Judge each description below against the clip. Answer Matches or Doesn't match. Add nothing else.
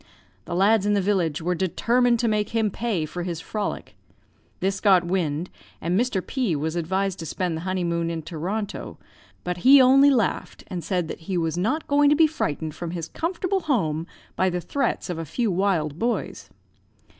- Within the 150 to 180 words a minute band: Doesn't match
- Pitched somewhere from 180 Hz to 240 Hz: Matches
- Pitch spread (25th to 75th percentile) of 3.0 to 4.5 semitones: Doesn't match